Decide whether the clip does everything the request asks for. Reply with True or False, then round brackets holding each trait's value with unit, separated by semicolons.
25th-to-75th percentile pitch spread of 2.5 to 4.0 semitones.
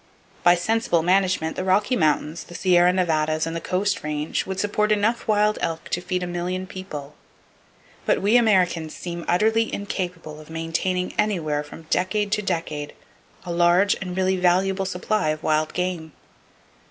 True (3.1 semitones)